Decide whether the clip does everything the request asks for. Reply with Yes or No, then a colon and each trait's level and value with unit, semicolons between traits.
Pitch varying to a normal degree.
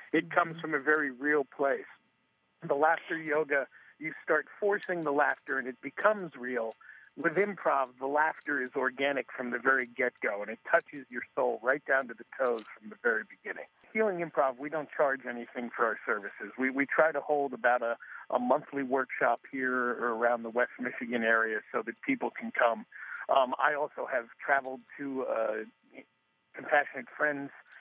Yes: average, 3.6 semitones